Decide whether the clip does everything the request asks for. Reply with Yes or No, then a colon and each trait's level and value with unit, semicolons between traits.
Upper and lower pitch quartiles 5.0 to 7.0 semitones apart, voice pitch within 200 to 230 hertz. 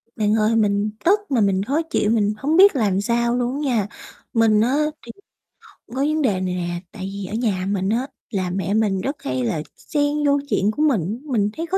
Yes: wide, 5.4 semitones; high, 220 Hz